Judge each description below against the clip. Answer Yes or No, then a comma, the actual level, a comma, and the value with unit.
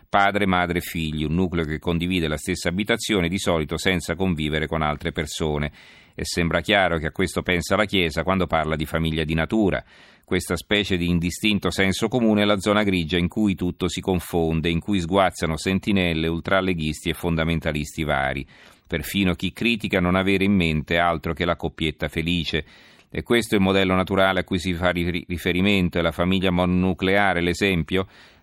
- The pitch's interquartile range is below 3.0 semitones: Yes, narrow, 2.6 semitones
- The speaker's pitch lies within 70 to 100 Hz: Yes, very low, 90 Hz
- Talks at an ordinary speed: No, fast, 175 wpm